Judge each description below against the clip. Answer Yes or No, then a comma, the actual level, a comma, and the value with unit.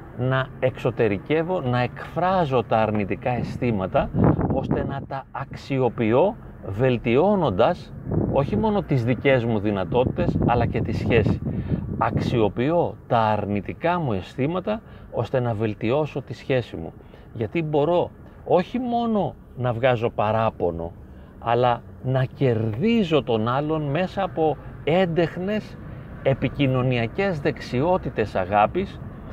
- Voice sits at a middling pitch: No, low, 125 Hz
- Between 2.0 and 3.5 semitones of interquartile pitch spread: No, average, 5.1 semitones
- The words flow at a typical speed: No, slow, 105 wpm